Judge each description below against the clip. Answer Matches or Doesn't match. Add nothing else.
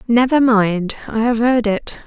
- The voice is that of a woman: Matches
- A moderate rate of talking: Matches